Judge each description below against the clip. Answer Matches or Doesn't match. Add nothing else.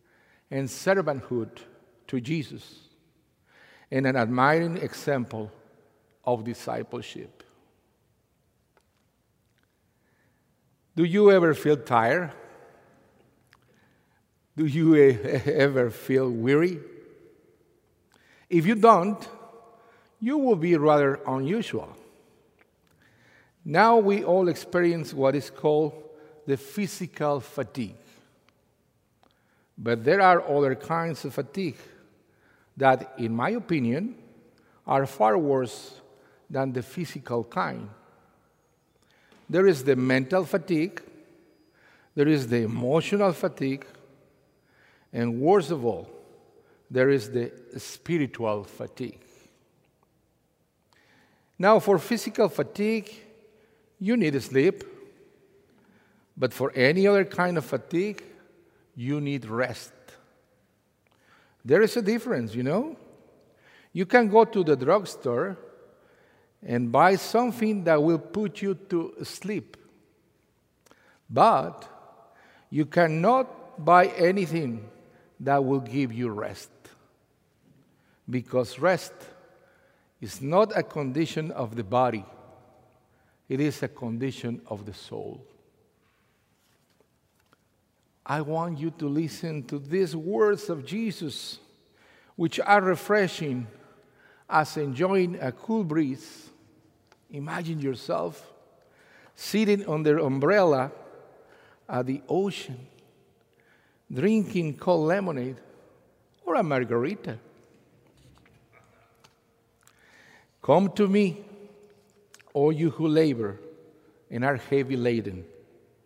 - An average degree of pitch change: Doesn't match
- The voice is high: Doesn't match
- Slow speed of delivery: Matches